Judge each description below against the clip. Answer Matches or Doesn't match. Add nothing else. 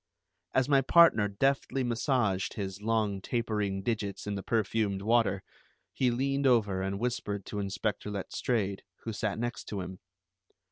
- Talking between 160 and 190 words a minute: Doesn't match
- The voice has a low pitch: Matches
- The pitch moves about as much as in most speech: Matches